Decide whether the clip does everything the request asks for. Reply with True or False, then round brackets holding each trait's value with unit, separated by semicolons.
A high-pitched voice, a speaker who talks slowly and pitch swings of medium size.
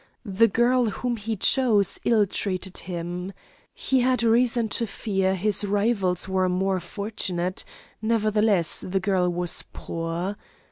True (200 Hz; 130 wpm; 3.5 semitones)